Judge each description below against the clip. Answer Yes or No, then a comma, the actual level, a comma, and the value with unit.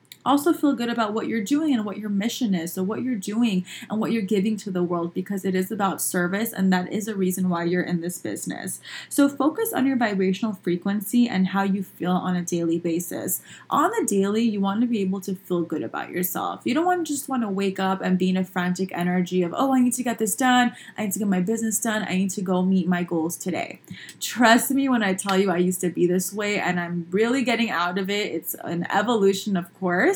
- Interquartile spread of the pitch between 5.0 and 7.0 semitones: No, average, 4.0 semitones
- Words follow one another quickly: Yes, fast, 255 wpm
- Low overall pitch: No, high, 195 Hz